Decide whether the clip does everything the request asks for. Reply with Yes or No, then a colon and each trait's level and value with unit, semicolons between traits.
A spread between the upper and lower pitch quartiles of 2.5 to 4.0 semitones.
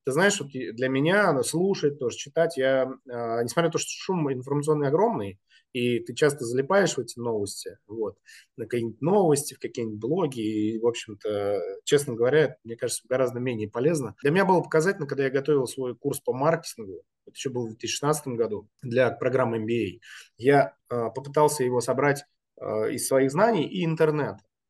No: average, 4.5 semitones